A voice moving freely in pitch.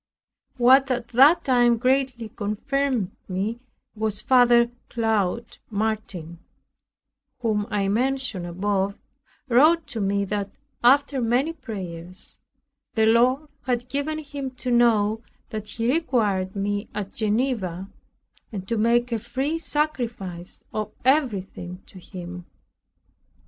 No: average, 4.3 semitones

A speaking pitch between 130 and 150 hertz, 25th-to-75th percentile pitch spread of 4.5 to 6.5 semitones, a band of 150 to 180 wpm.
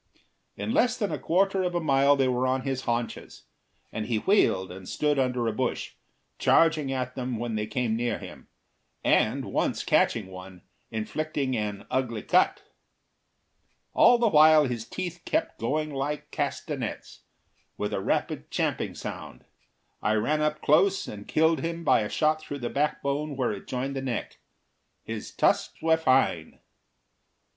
Yes: low, 135 Hz; average, 4.9 semitones; average, 160 wpm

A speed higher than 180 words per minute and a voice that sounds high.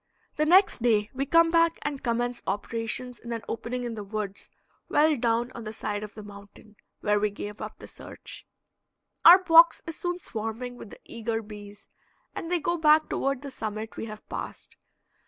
Yes: average, 190 wpm; high, 235 Hz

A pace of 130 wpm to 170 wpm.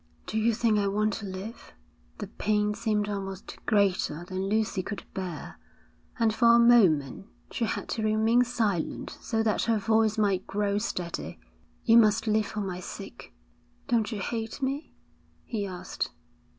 Yes: average, 160 wpm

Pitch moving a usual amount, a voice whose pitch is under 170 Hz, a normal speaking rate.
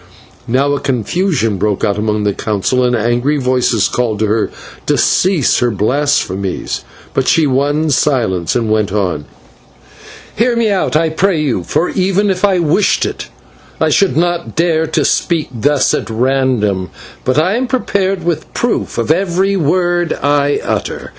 No: wide, 7.7 semitones; medium, 140 Hz; average, 160 wpm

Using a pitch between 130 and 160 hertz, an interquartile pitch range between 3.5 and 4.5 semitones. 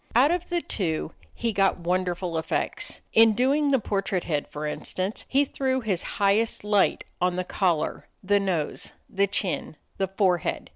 No: high, 195 Hz; average, 4.1 semitones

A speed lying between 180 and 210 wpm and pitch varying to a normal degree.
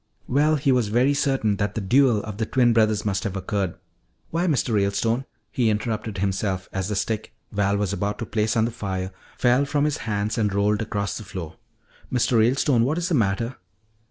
Yes: average, 200 wpm; average, 3.5 semitones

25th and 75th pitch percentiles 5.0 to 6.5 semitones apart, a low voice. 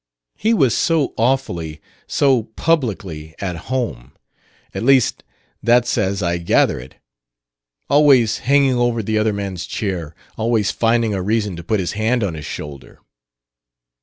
Yes: wide, 5.6 semitones; low, 110 Hz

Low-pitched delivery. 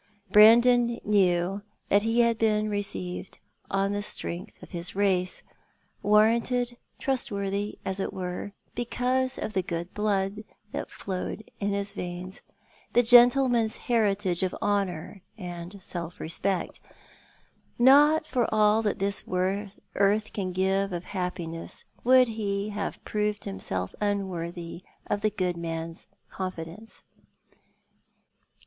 No: high, 200 Hz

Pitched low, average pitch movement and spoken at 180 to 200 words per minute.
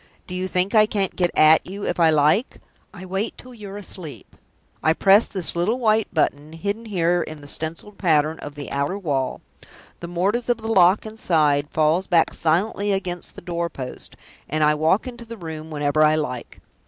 No: medium, 175 Hz; average, 4.6 semitones; average, 190 wpm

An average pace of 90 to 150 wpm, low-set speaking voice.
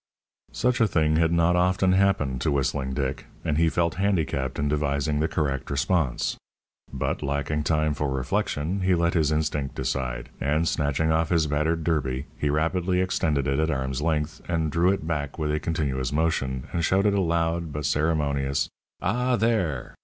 No: average, 175 wpm; very low, 75 Hz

